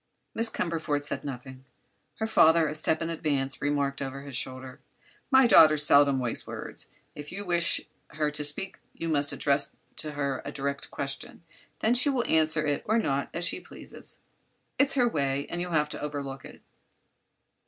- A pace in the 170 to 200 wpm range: Yes, average, 175 wpm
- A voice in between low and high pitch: Yes, medium, 150 Hz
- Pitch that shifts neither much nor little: Yes, average, 3.2 semitones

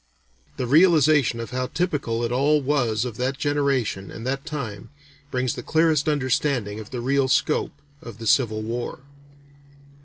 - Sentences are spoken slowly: No, average, 155 wpm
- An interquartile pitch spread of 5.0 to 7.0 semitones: No, average, 3.9 semitones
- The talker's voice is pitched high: No, low, 130 Hz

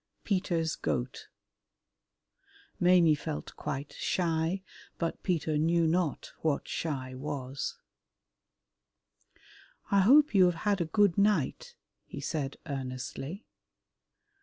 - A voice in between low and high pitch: Yes, medium, 165 Hz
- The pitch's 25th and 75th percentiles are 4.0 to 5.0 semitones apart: Yes, average, 4.7 semitones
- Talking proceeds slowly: Yes, slow, 100 wpm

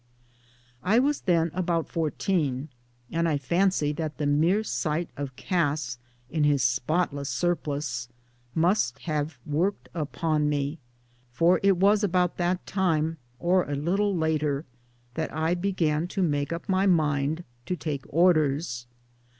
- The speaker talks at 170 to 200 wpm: No, slow, 135 wpm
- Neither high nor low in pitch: Yes, medium, 160 Hz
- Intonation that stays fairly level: No, average, 3.6 semitones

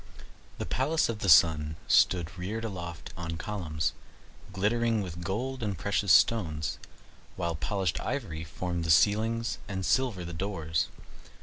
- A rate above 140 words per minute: No, slow, 135 wpm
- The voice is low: Yes, very low, 95 Hz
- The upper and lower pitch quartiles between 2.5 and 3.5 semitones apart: No, average, 4.8 semitones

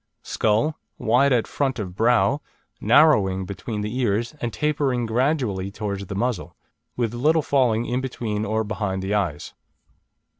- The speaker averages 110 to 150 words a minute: Yes, average, 145 wpm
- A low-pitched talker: Yes, low, 115 Hz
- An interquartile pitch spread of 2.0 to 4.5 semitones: Yes, average, 4.1 semitones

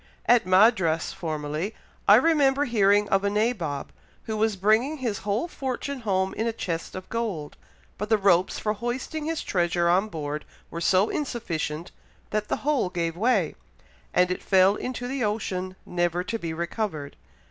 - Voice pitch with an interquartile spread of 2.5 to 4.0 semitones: No, average, 5.1 semitones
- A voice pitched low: No, high, 200 Hz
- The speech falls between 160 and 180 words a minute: Yes, average, 165 wpm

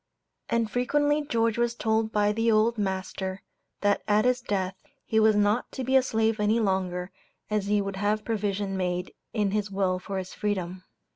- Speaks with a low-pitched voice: No, high, 210 Hz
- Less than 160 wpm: No, average, 185 wpm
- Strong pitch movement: No, average, 2.8 semitones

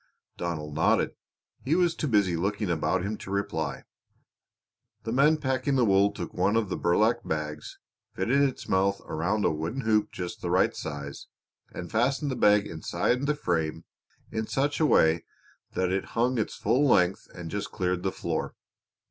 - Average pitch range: No, wide, 6.2 semitones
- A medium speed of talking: Yes, average, 175 wpm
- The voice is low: Yes, low, 100 Hz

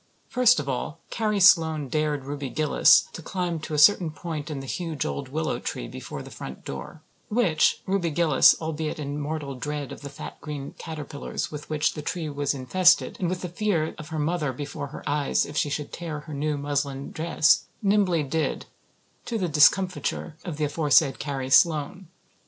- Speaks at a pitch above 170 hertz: No, medium, 155 Hz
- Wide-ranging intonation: No, average, 2.9 semitones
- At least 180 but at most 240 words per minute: Yes, average, 185 wpm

